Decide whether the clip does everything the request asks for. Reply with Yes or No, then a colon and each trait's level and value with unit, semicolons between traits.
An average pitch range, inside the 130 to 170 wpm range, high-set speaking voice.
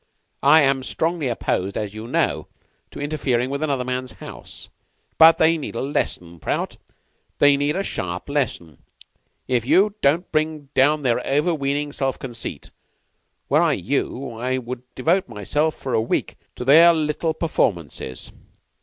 No: average, 4.1 semitones; average, 155 wpm; medium, 140 Hz